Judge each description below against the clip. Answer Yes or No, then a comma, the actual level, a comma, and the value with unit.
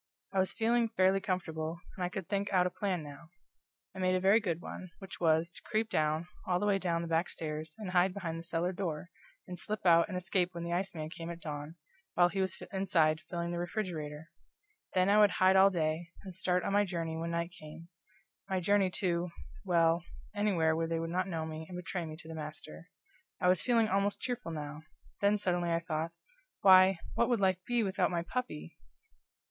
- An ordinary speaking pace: No, fast, 210 wpm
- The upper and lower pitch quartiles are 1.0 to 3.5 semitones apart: Yes, average, 2.7 semitones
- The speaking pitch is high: No, medium, 175 Hz